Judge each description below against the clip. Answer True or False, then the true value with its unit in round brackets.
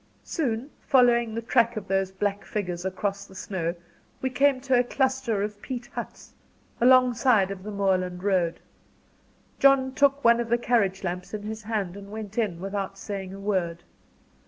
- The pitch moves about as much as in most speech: True (4.0 semitones)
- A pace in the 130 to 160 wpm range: False (170 wpm)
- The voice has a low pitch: False (210 Hz)